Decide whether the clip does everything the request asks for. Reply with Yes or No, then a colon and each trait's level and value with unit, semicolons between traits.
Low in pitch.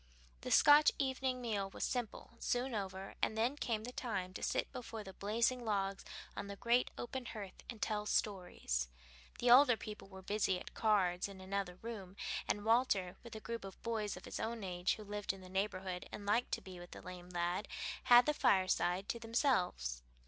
No: high, 205 Hz